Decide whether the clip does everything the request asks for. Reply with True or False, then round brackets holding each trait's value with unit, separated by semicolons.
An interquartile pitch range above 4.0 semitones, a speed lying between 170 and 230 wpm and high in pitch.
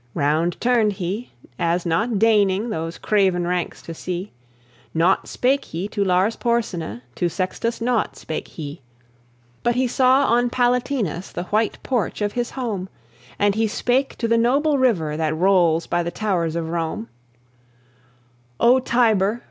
False (5.6 semitones; 150 wpm; 205 Hz)